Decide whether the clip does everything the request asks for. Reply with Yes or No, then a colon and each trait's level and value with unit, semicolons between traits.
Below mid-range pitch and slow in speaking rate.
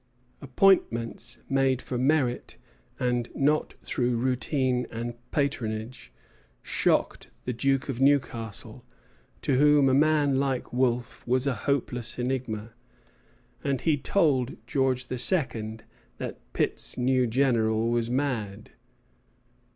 Yes: low, 125 Hz; slow, 110 wpm